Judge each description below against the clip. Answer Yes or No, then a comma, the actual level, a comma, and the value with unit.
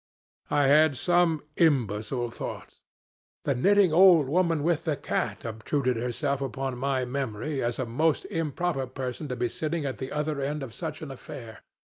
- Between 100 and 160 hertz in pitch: Yes, medium, 140 Hz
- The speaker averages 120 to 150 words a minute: No, average, 165 wpm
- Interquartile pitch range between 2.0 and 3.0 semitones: No, average, 4.0 semitones